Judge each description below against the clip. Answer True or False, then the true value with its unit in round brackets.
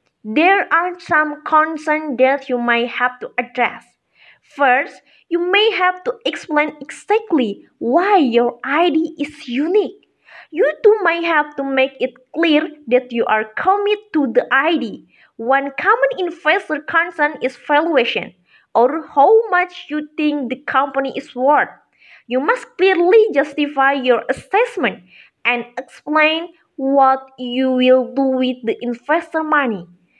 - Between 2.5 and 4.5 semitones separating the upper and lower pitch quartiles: False (4.9 semitones)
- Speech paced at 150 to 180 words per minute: False (135 wpm)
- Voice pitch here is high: True (295 Hz)